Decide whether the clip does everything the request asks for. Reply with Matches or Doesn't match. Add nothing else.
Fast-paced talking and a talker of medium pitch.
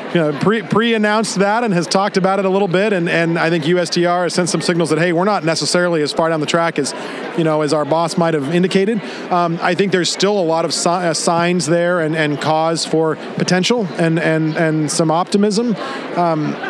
Matches